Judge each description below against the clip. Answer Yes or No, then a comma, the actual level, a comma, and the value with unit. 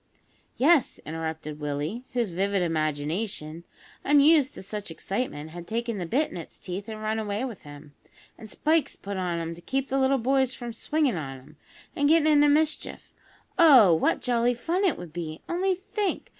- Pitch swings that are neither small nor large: No, wide, 8.7 semitones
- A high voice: Yes, high, 220 Hz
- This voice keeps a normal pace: Yes, average, 180 wpm